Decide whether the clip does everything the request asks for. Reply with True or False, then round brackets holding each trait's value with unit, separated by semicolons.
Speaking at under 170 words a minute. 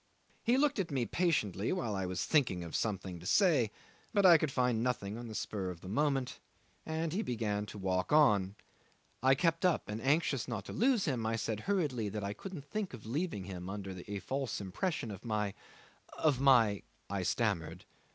False (195 wpm)